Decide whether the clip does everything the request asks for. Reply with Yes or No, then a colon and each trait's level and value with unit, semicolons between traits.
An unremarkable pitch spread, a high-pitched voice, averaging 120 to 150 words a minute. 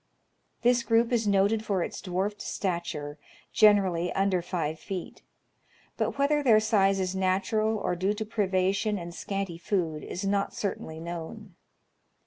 Yes: average, 3.3 semitones; high, 195 Hz; average, 140 wpm